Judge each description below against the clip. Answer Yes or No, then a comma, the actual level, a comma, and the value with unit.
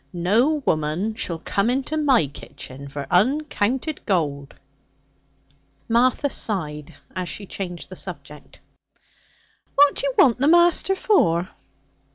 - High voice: Yes, high, 205 Hz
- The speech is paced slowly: Yes, slow, 120 wpm